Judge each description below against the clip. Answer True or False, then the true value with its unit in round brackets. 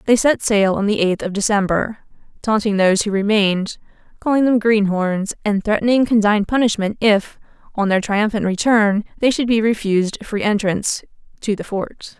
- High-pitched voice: True (210 Hz)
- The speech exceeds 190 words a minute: False (160 wpm)